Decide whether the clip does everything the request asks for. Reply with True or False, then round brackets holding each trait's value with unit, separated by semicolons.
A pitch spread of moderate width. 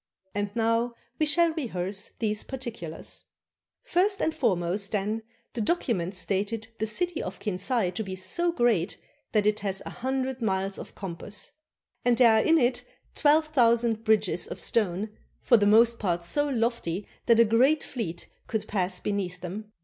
True (4.2 semitones)